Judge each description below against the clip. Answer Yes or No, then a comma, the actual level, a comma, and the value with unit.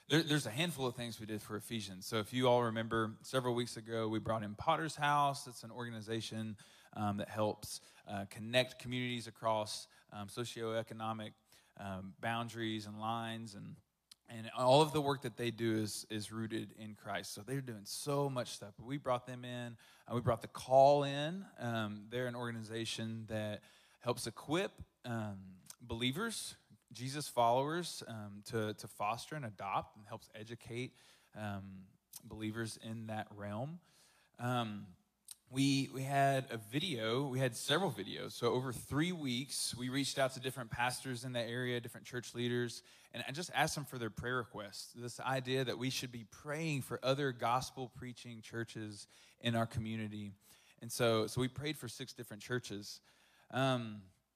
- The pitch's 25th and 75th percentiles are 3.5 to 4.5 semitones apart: No, average, 2.9 semitones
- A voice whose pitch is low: Yes, low, 120 Hz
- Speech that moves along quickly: No, average, 170 wpm